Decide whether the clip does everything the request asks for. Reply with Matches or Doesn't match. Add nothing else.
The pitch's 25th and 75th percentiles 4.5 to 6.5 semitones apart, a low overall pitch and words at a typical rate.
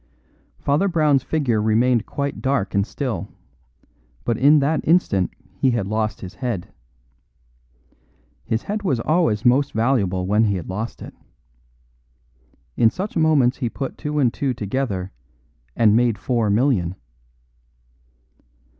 Doesn't match